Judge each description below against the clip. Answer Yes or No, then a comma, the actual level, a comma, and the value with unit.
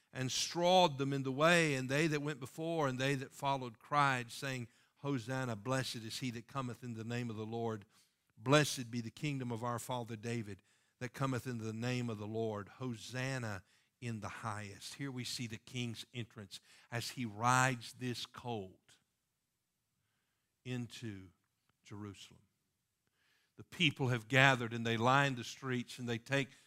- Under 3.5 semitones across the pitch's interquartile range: Yes, narrow, 2.6 semitones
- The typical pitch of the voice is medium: No, low, 125 Hz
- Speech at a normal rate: Yes, average, 165 wpm